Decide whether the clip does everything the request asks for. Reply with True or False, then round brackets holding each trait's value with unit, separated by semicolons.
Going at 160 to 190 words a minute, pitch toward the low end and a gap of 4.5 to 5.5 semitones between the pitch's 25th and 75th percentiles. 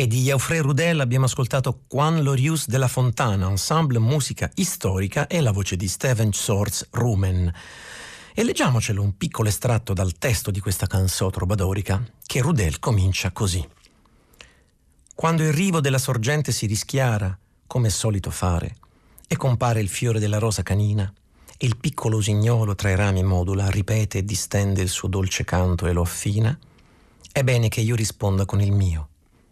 True (165 wpm; 105 Hz; 5.0 semitones)